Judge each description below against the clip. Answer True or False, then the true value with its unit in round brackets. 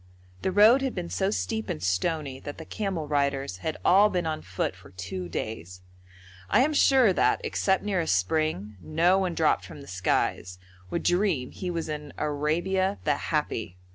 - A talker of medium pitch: True (155 Hz)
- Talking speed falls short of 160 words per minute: False (180 wpm)